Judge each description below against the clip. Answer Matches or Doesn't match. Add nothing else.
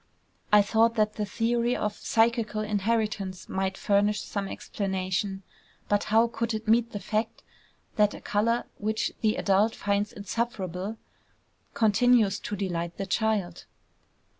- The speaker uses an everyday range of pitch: Doesn't match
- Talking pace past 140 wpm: Doesn't match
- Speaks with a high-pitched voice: Matches